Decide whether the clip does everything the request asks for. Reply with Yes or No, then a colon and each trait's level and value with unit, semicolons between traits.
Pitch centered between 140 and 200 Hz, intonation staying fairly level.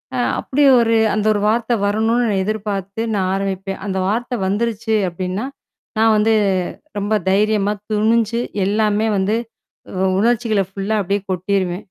No: high, 210 Hz; narrow, 2.2 semitones